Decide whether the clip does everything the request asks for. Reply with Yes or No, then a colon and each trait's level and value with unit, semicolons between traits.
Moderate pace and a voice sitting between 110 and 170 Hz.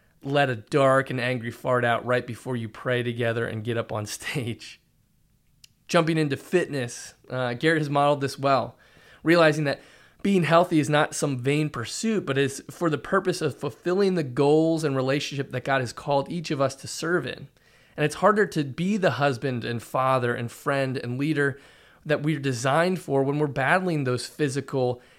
Yes: average, 185 wpm; medium, 140 Hz